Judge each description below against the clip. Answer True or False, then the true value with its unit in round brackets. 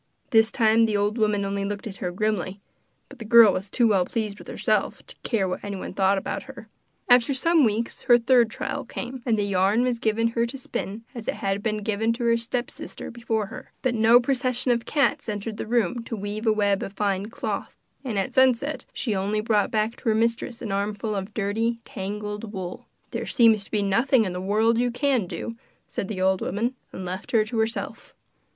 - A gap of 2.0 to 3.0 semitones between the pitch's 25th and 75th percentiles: True (2.7 semitones)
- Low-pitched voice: False (220 Hz)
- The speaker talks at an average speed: False (210 wpm)